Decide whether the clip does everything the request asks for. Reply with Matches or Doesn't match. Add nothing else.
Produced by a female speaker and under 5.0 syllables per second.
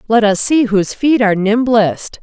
Matches